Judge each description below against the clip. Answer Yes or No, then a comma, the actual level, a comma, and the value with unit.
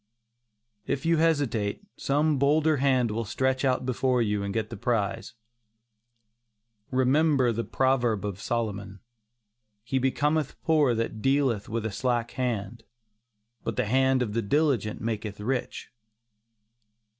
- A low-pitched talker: Yes, low, 125 Hz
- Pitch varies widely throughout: No, average, 3.6 semitones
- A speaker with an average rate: No, slow, 130 wpm